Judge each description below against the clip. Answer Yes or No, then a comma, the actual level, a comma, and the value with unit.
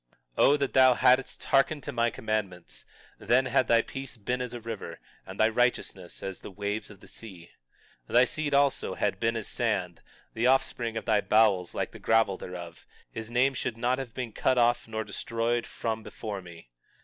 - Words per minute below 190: No, average, 195 wpm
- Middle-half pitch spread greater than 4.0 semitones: No, average, 3.5 semitones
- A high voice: No, low, 115 Hz